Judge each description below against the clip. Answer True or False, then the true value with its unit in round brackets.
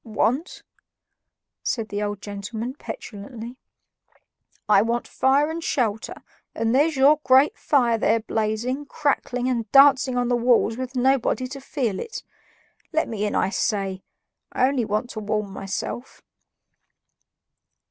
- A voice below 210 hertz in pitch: False (240 Hz)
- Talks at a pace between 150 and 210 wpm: False (135 wpm)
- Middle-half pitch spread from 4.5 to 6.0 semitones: False (3.8 semitones)